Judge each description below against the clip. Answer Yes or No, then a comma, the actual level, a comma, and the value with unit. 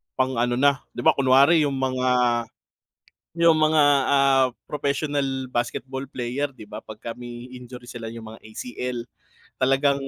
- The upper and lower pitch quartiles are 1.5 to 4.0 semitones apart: Yes, narrow, 2.6 semitones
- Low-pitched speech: Yes, low, 130 Hz